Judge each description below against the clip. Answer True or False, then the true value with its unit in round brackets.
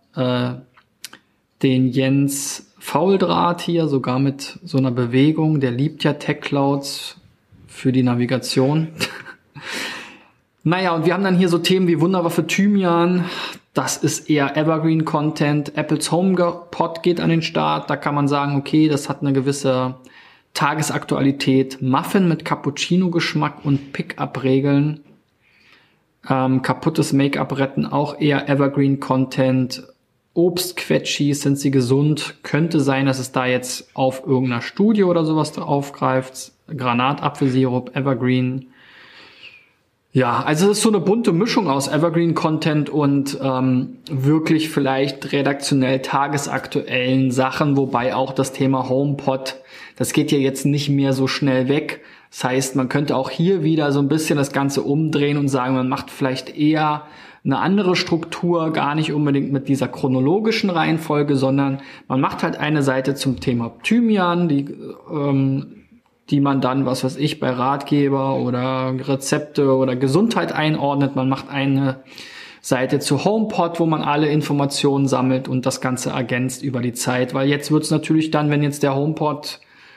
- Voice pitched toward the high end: False (140 Hz)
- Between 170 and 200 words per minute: False (145 wpm)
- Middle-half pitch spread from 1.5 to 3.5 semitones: True (2.7 semitones)